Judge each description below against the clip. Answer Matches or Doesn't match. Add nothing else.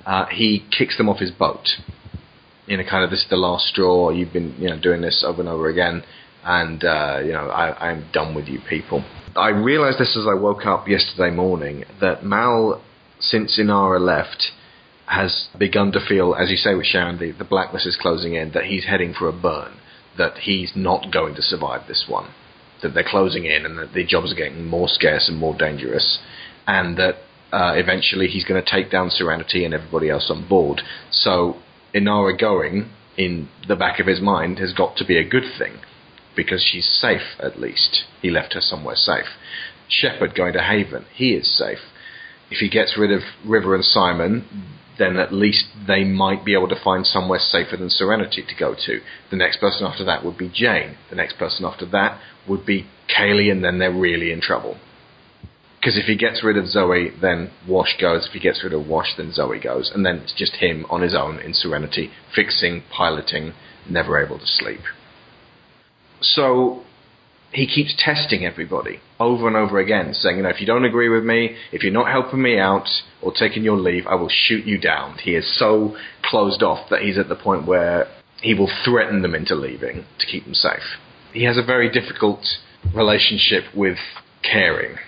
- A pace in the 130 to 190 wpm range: Doesn't match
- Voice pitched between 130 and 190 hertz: Doesn't match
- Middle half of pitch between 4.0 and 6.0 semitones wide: Doesn't match